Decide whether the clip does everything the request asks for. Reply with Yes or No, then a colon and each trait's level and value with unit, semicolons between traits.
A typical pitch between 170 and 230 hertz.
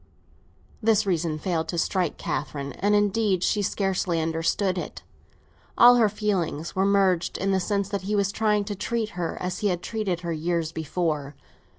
Yes: medium, 185 Hz